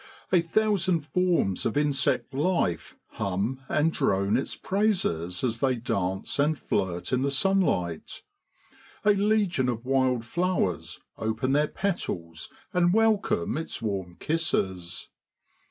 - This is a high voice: No, low, 135 Hz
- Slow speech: Yes, slow, 120 wpm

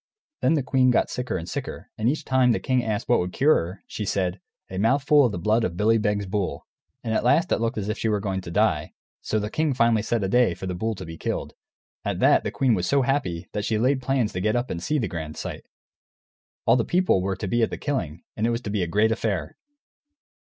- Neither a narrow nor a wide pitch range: Yes, average, 4.8 semitones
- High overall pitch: No, low, 110 Hz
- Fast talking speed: Yes, fast, 260 wpm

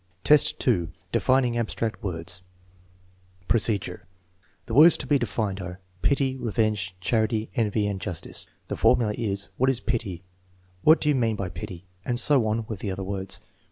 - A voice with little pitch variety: No, average, 4.1 semitones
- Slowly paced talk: No, average, 165 wpm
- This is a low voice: Yes, low, 110 Hz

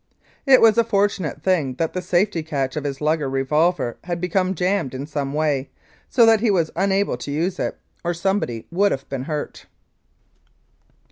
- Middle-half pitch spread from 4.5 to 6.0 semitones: Yes, average, 5.3 semitones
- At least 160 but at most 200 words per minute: Yes, average, 180 wpm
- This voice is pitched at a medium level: Yes, medium, 165 Hz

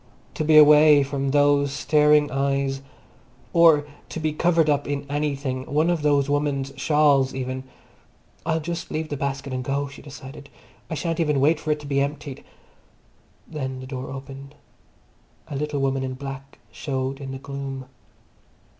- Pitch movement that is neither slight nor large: No, narrow, 1.8 semitones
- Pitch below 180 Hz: Yes, medium, 140 Hz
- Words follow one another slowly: No, average, 165 wpm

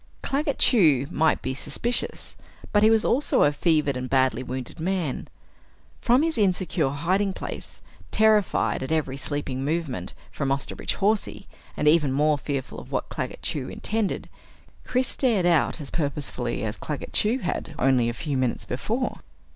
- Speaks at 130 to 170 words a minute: Yes, average, 155 wpm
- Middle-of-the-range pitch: Yes, medium, 155 Hz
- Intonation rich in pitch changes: Yes, wide, 7.5 semitones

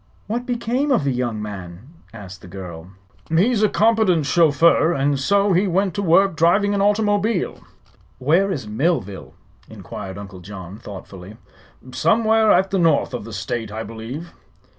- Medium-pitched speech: Yes, medium, 160 Hz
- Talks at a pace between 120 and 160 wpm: Yes, average, 155 wpm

